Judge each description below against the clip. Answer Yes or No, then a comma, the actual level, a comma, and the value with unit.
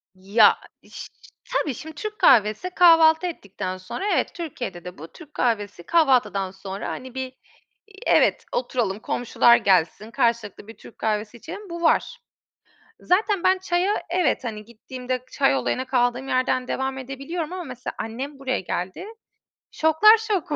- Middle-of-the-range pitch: No, very high, 255 Hz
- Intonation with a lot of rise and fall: Yes, wide, 7.3 semitones